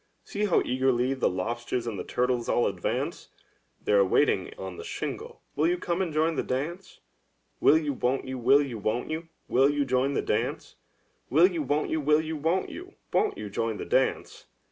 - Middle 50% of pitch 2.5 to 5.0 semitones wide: Yes, average, 4.7 semitones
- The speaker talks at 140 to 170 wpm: No, fast, 205 wpm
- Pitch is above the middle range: No, low, 135 Hz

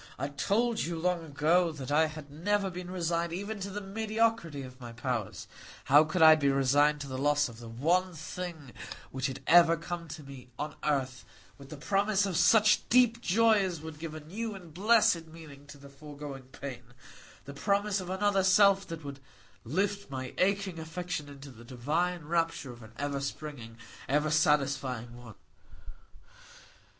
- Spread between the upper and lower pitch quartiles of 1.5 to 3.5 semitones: No, average, 5.0 semitones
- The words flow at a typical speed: Yes, average, 175 wpm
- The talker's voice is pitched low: No, medium, 155 Hz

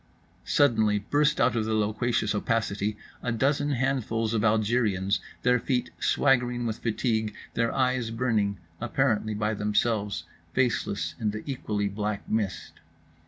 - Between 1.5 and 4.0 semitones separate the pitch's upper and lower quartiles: Yes, average, 2.8 semitones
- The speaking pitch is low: Yes, low, 110 Hz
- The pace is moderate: No, slow, 125 wpm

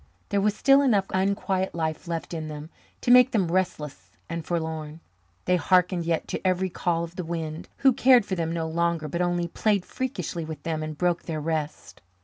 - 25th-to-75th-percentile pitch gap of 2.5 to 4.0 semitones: Yes, average, 2.8 semitones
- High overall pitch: No, medium, 170 Hz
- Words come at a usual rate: Yes, average, 195 wpm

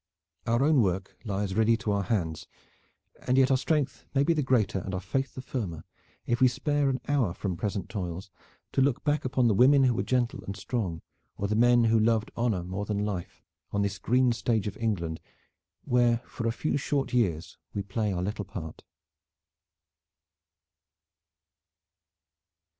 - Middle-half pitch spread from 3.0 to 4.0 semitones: No, average, 4.6 semitones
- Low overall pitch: Yes, low, 110 Hz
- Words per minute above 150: Yes, average, 175 wpm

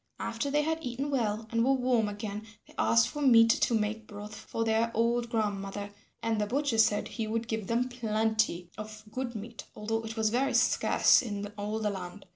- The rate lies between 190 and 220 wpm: Yes, average, 200 wpm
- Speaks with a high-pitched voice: Yes, high, 220 Hz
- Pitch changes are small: Yes, narrow, 2.1 semitones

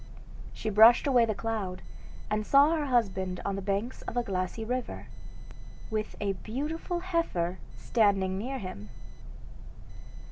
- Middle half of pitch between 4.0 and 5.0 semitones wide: Yes, average, 4.7 semitones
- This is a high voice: Yes, high, 215 Hz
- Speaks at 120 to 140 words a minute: Yes, slow, 135 wpm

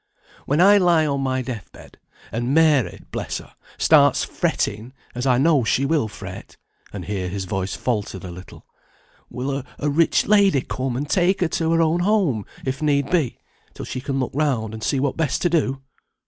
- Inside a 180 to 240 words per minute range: Yes, average, 190 wpm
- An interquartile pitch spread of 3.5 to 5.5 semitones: Yes, average, 5.2 semitones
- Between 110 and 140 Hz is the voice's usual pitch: Yes, low, 135 Hz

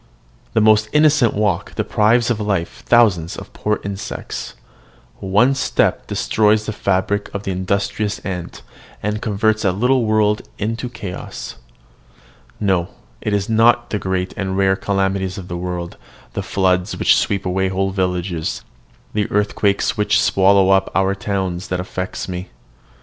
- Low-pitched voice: Yes, low, 100 Hz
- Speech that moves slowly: No, average, 145 wpm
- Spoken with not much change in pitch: Yes, narrow, 2.3 semitones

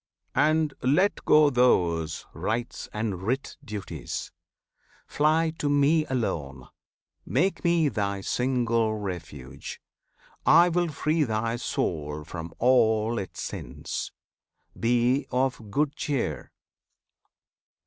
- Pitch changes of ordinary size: No, wide, 7.0 semitones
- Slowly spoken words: Yes, slow, 100 wpm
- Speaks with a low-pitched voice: Yes, low, 120 Hz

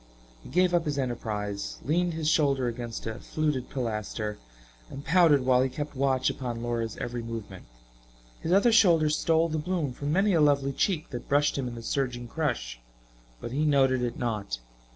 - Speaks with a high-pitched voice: No, low, 135 Hz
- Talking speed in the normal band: Yes, average, 180 wpm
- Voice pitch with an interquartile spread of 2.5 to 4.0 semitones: No, average, 4.6 semitones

